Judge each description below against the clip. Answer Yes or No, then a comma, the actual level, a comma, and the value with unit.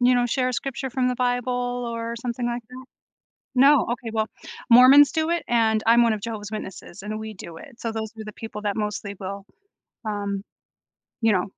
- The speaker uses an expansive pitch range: No, average, 2.7 semitones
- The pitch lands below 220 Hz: No, high, 230 Hz